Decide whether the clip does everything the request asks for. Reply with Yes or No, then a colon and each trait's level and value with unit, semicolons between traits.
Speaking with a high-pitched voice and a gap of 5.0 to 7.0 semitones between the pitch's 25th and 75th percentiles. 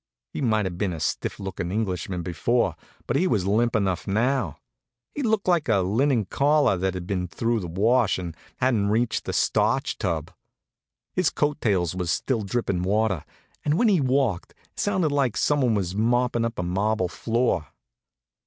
No: low, 110 Hz; wide, 5.6 semitones